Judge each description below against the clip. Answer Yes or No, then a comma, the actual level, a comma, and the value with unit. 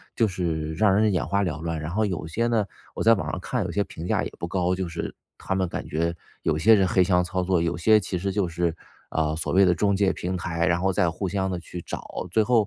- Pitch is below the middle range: Yes, very low, 90 Hz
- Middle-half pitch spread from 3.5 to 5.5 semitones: No, average, 2.8 semitones